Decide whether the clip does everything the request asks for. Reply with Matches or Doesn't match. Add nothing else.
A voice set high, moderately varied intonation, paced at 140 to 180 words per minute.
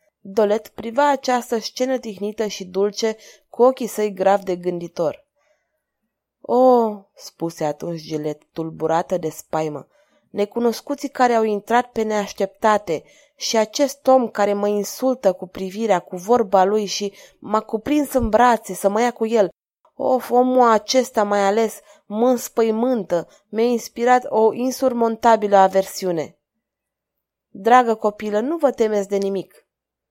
Doesn't match